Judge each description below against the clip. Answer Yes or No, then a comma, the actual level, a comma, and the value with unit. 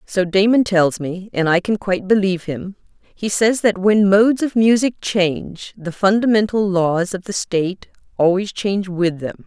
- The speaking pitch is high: Yes, high, 195 Hz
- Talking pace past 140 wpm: Yes, average, 170 wpm